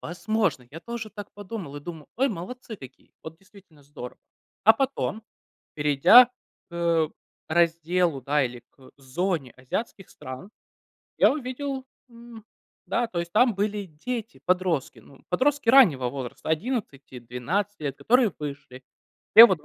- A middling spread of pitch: No, wide, 7.6 semitones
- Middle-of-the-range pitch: Yes, medium, 180 Hz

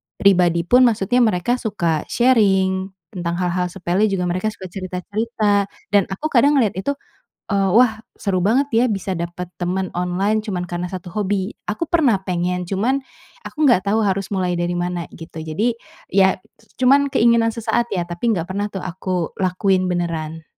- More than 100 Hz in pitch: Yes, high, 190 Hz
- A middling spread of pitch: Yes, average, 3.7 semitones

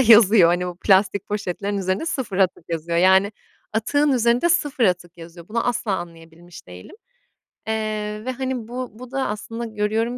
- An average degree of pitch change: Yes, average, 4.9 semitones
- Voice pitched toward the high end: Yes, high, 210 Hz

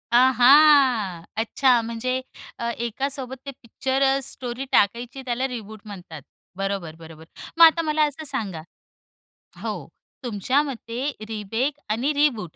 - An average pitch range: Yes, average, 4.2 semitones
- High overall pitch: Yes, high, 245 Hz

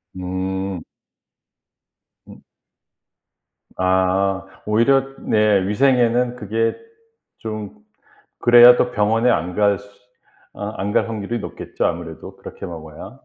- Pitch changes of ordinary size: Yes, average, 3.7 semitones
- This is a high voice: No, low, 105 Hz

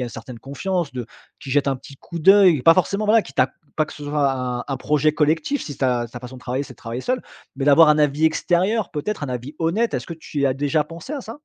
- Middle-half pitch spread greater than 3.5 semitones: Yes, average, 4.4 semitones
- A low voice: No, medium, 150 Hz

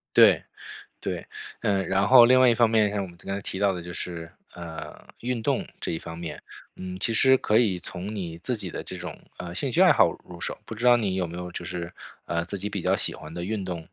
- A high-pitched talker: No, very low, 95 Hz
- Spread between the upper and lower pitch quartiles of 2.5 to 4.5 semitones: Yes, average, 4.0 semitones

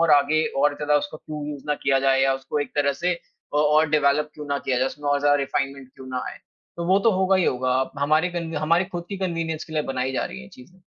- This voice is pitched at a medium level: Yes, medium, 145 Hz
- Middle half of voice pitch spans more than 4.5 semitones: No, narrow, 2.6 semitones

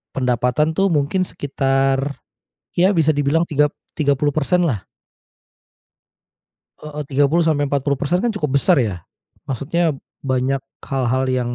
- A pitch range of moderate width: Yes, average, 3.0 semitones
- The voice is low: No, medium, 145 Hz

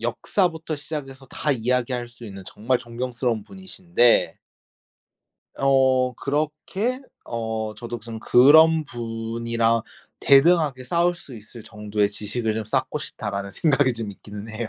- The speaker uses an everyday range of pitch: Yes, average, 4.3 semitones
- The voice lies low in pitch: Yes, low, 120 Hz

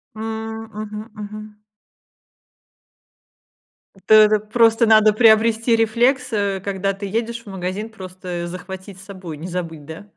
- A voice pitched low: No, high, 210 Hz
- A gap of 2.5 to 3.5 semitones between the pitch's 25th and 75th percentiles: Yes, average, 2.8 semitones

